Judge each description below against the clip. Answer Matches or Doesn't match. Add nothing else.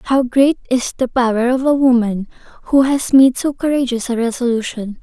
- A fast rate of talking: Doesn't match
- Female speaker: Matches